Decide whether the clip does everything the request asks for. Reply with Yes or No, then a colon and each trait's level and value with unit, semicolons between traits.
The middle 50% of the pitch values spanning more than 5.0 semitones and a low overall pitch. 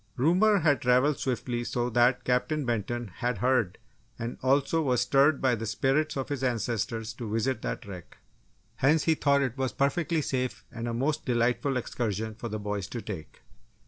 No: average, 3.2 semitones; low, 125 Hz